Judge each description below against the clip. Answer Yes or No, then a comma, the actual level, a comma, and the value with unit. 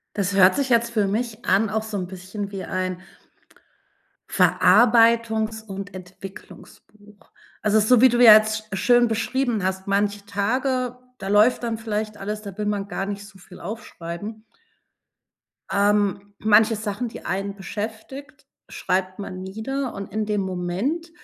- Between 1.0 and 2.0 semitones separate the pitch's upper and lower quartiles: No, narrow, 2.4 semitones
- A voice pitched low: No, high, 210 Hz